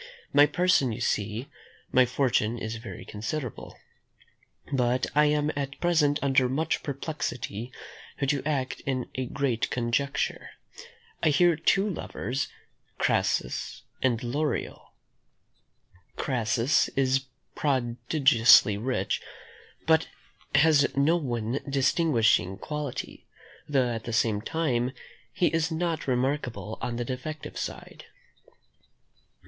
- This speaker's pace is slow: Yes, slow, 110 wpm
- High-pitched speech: No, low, 135 Hz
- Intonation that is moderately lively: Yes, average, 3.9 semitones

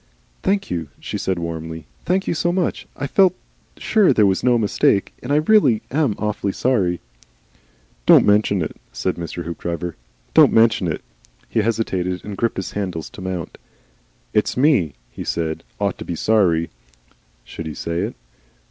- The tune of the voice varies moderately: No, wide, 6.4 semitones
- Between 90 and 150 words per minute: No, average, 165 wpm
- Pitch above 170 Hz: No, low, 100 Hz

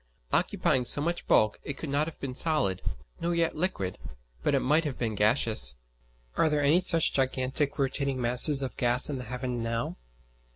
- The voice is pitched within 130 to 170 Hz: Yes, low, 135 Hz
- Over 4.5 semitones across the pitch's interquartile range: No, average, 3.9 semitones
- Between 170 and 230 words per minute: Yes, average, 180 wpm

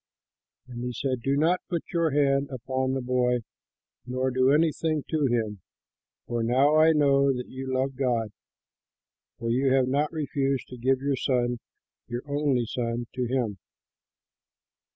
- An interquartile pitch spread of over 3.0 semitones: No, narrow, 2.4 semitones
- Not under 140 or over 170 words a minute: Yes, average, 150 wpm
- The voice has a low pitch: Yes, low, 130 Hz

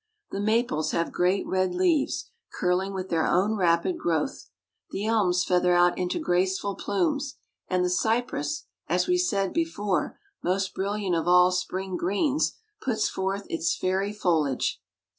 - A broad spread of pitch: No, average, 3.6 semitones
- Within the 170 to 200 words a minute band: No, average, 145 wpm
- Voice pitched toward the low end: No, high, 190 Hz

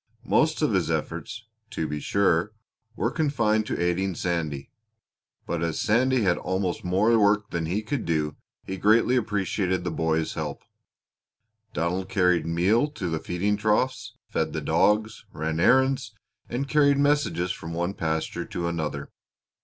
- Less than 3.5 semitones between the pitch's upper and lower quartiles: No, average, 4.8 semitones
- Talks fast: No, average, 150 wpm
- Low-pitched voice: Yes, very low, 95 Hz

